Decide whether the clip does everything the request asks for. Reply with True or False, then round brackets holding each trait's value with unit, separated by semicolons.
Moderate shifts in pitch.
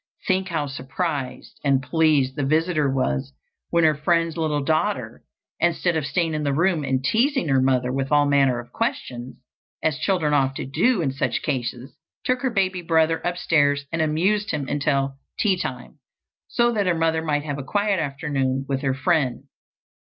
True (4.0 semitones)